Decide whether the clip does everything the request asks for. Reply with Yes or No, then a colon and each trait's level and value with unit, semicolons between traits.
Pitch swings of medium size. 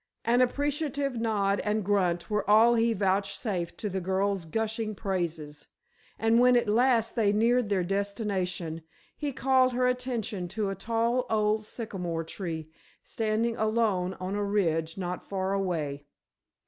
Yes: average, 3.8 semitones